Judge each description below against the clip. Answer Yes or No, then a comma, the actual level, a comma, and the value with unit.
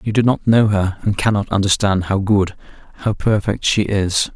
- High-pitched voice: No, low, 100 Hz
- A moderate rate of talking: Yes, average, 195 wpm